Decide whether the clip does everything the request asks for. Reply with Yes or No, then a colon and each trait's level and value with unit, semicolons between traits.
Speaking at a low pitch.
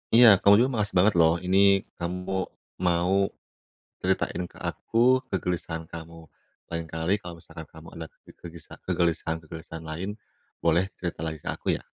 Yes: very low, 85 Hz